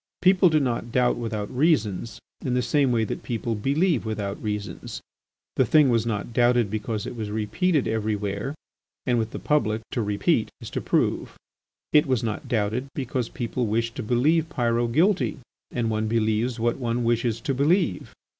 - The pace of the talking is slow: No, average, 175 wpm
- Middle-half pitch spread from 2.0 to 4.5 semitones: Yes, average, 3.5 semitones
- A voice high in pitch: No, low, 120 Hz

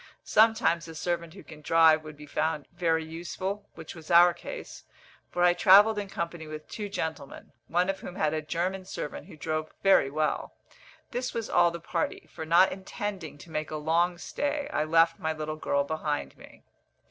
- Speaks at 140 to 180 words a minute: No, average, 190 wpm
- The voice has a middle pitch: Yes, medium, 165 Hz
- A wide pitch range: No, average, 3.1 semitones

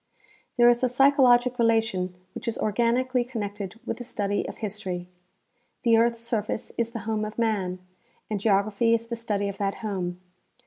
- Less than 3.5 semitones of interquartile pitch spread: Yes, average, 2.8 semitones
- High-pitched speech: Yes, high, 225 Hz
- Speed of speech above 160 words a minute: Yes, average, 170 wpm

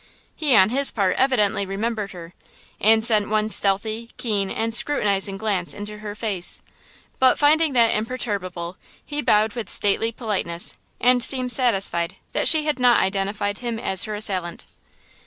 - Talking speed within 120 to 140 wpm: No, average, 155 wpm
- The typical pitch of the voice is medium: No, high, 215 Hz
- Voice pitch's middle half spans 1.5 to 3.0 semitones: No, average, 3.6 semitones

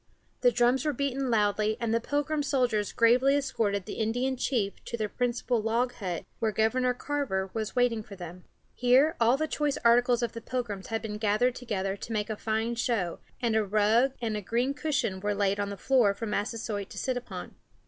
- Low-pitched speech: No, high, 230 Hz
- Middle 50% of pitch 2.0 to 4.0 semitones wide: Yes, average, 3.2 semitones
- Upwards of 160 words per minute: Yes, average, 200 wpm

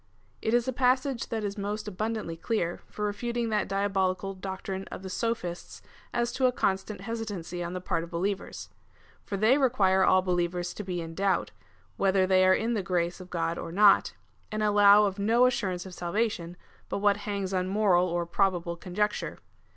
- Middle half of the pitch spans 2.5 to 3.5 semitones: Yes, average, 2.9 semitones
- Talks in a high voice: Yes, high, 195 Hz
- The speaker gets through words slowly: No, average, 185 wpm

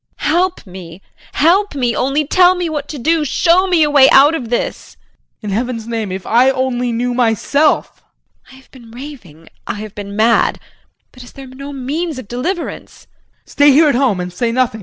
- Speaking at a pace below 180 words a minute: No, fast, 205 wpm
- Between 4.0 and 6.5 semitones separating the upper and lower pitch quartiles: Yes, average, 4.6 semitones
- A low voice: No, very high, 260 Hz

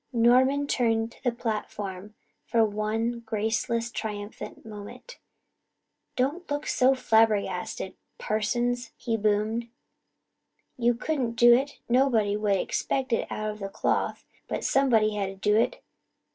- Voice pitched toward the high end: Yes, high, 225 Hz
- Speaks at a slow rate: Yes, slow, 125 wpm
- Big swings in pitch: No, narrow, 2.5 semitones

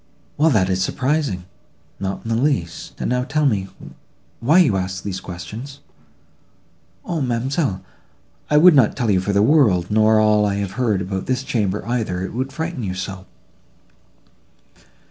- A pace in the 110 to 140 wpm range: No, average, 160 wpm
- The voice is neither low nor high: No, low, 110 Hz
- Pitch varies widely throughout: Yes, wide, 5.9 semitones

